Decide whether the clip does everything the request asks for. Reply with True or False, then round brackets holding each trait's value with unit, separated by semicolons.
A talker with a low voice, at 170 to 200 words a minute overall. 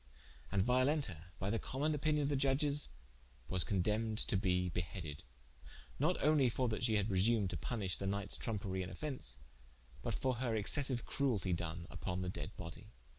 True (110 Hz; 175 wpm)